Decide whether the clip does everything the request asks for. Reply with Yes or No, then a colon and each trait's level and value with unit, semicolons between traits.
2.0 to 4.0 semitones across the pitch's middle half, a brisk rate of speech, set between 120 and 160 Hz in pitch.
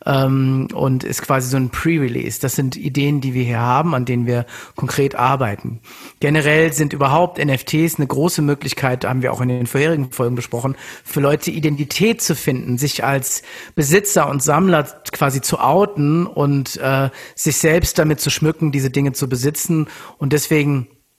No: average, 2.7 semitones; average, 165 wpm; medium, 140 Hz